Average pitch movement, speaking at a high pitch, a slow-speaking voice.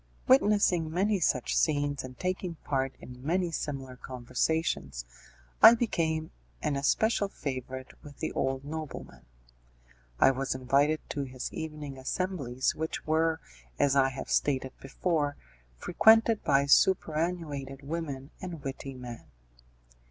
No: average, 3.8 semitones; medium, 145 Hz; slow, 120 wpm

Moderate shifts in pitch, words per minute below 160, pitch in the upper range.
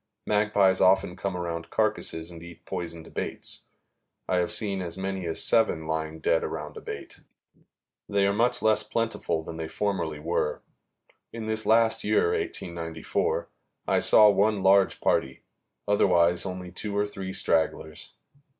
No: average, 3.8 semitones; average, 150 wpm; very low, 95 Hz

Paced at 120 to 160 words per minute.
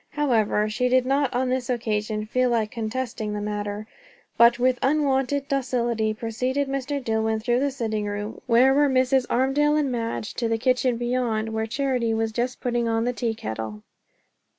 No: average, 175 wpm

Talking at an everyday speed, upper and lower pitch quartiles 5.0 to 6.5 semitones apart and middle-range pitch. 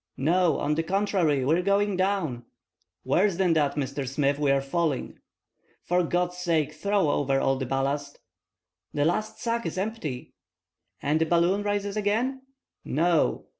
Yes: average, 155 wpm; wide, 5.6 semitones; medium, 165 Hz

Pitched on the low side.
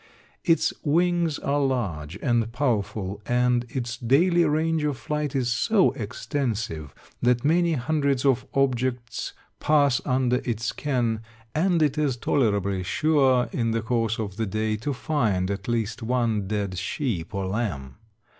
Yes: low, 125 Hz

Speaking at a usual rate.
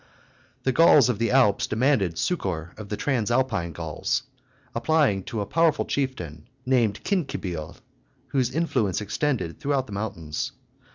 No: slow, 130 wpm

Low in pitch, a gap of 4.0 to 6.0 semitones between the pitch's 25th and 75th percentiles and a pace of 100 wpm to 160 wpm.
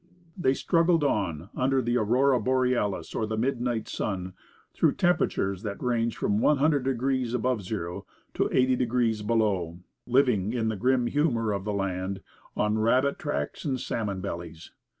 Yes: low, 115 Hz; average, 4.3 semitones; average, 155 wpm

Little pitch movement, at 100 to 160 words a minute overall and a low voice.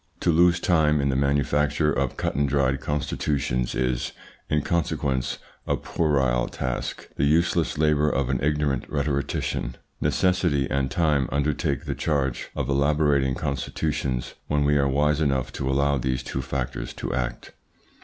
Yes: narrow, 2.1 semitones; average, 150 wpm; very low, 70 Hz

